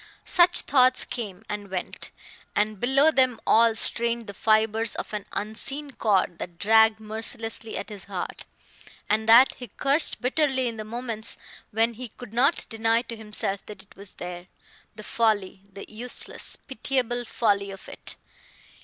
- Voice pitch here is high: Yes, high, 225 Hz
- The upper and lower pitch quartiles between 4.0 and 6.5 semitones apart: No, average, 2.8 semitones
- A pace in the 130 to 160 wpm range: Yes, average, 155 wpm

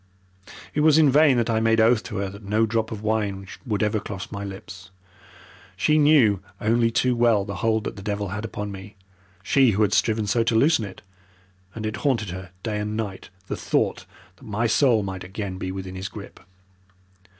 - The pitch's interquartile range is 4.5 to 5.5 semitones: No, narrow, 2.6 semitones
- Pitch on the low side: Yes, low, 105 Hz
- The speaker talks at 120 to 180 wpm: No, fast, 205 wpm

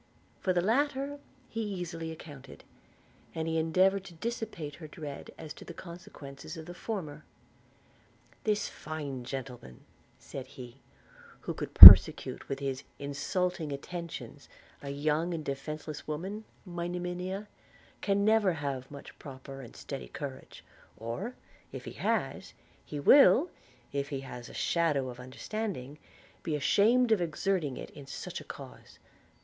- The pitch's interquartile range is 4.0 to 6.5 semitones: Yes, average, 5.1 semitones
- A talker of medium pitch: Yes, medium, 160 Hz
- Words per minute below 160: Yes, average, 140 wpm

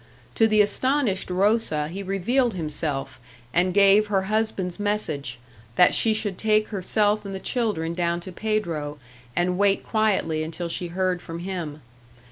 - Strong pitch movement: No, average, 3.9 semitones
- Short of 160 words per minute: Yes, average, 150 wpm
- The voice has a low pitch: No, high, 190 Hz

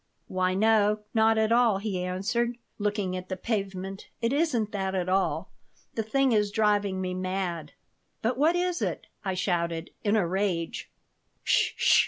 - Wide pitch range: No, average, 3.2 semitones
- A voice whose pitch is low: No, high, 205 Hz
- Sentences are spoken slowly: No, average, 165 wpm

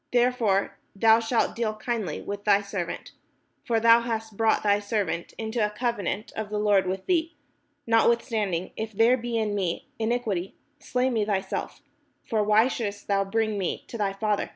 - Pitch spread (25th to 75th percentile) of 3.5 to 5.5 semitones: No, narrow, 2.4 semitones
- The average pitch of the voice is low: No, high, 215 Hz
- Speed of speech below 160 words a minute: No, average, 175 wpm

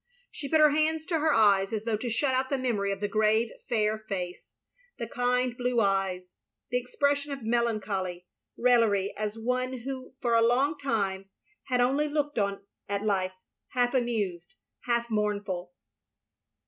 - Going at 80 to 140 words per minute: No, average, 170 wpm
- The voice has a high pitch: Yes, high, 230 Hz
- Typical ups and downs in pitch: Yes, average, 4.1 semitones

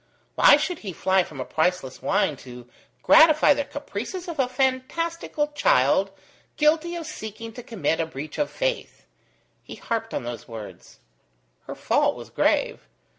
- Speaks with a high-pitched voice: Yes, high, 230 Hz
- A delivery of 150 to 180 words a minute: Yes, average, 155 wpm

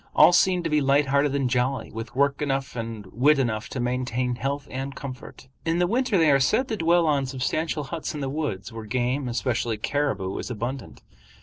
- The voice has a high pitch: No, low, 135 Hz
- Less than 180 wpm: No, fast, 205 wpm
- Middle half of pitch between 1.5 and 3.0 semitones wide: No, average, 3.4 semitones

